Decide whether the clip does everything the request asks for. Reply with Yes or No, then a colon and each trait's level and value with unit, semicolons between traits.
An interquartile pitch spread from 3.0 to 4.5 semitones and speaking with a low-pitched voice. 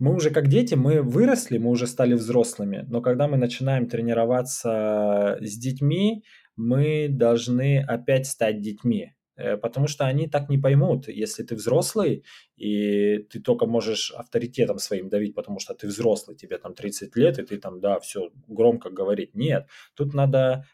Yes: average, 3.8 semitones; low, 120 Hz